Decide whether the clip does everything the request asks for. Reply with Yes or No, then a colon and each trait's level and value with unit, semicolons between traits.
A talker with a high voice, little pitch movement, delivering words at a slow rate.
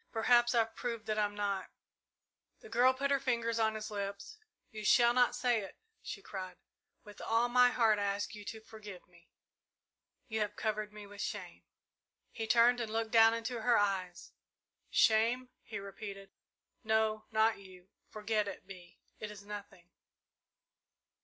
No: high, 220 Hz; narrow, 2.3 semitones; average, 165 wpm